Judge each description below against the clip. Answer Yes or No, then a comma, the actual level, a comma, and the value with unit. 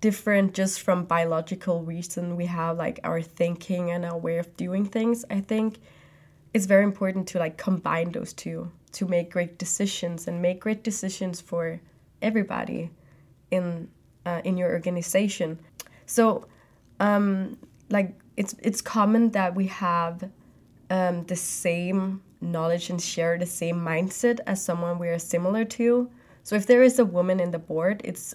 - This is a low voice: No, medium, 180 Hz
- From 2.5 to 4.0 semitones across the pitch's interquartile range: Yes, average, 2.9 semitones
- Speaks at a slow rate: No, average, 160 wpm